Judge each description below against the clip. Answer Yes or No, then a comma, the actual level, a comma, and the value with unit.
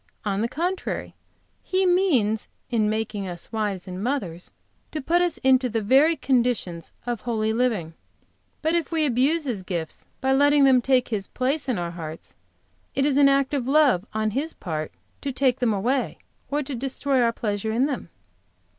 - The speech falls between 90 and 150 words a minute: No, average, 180 wpm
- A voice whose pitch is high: Yes, very high, 250 Hz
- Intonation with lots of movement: No, average, 4.9 semitones